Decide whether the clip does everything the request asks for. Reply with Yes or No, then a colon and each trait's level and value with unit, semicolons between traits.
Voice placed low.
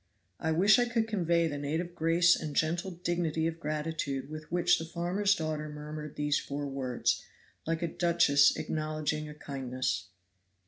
No: medium, 155 Hz